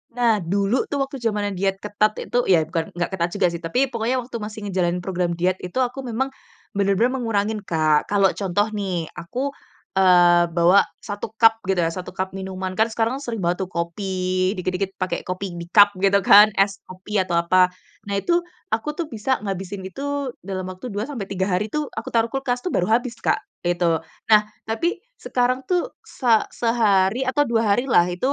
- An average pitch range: Yes, average, 3.8 semitones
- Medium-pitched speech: No, high, 200 Hz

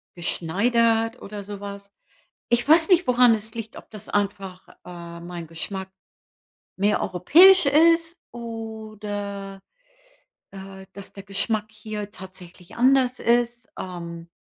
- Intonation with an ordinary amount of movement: Yes, average, 3.6 semitones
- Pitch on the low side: No, high, 205 Hz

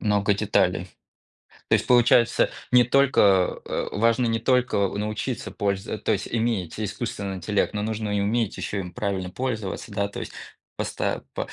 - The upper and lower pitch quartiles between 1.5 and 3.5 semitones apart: Yes, average, 2.7 semitones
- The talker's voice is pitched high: No, low, 105 Hz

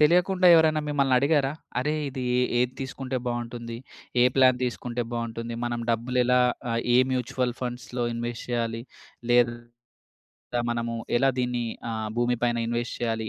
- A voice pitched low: Yes, low, 120 Hz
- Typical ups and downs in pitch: No, narrow, 1.6 semitones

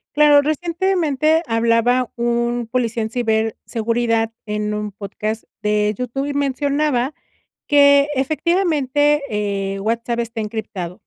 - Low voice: No, high, 240 Hz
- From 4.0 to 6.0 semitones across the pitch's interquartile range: Yes, average, 4.6 semitones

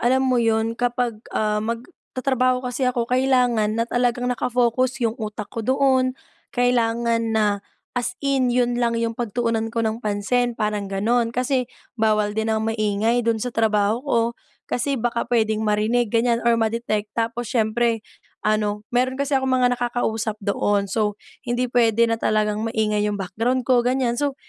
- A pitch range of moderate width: No, narrow, 2.2 semitones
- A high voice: Yes, high, 230 Hz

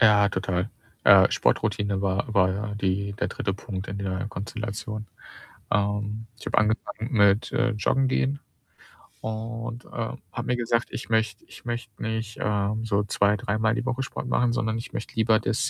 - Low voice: Yes, low, 110 Hz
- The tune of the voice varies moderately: No, narrow, 2.2 semitones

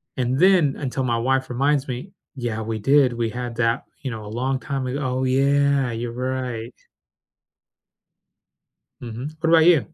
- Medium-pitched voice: No, low, 130 Hz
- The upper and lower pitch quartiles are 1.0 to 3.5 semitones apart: Yes, narrow, 2.6 semitones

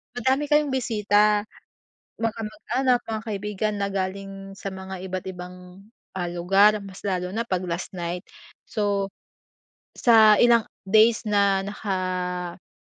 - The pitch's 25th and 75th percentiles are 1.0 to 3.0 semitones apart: Yes, narrow, 2.6 semitones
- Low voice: No, high, 200 Hz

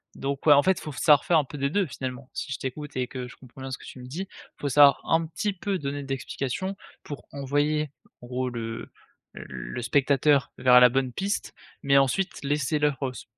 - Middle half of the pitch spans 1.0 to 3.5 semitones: Yes, average, 2.7 semitones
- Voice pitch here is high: No, medium, 140 Hz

